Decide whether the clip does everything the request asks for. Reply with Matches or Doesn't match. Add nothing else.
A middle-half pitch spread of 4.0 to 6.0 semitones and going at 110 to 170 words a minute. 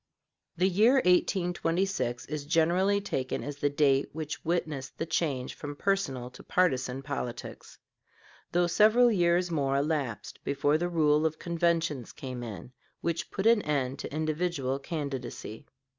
Matches